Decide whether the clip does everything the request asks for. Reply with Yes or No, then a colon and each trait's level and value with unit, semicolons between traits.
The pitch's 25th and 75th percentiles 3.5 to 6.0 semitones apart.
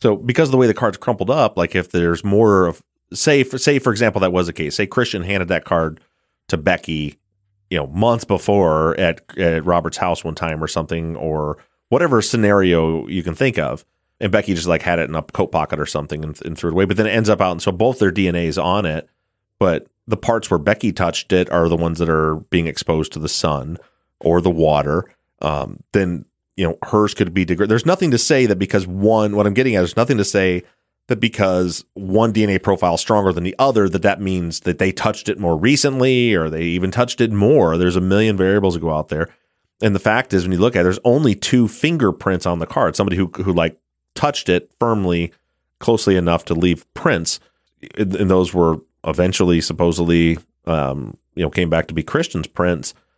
Yes: average, 3.8 semitones